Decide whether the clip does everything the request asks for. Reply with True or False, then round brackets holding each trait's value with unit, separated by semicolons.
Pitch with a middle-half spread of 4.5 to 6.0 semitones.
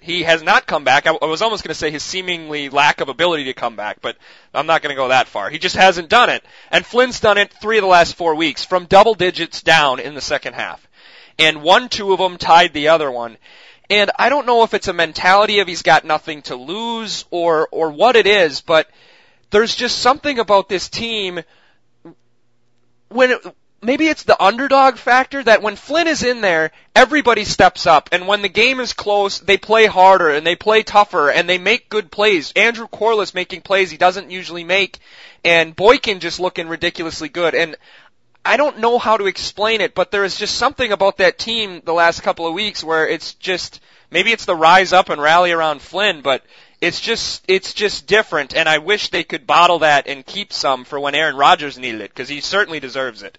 True (5.0 semitones)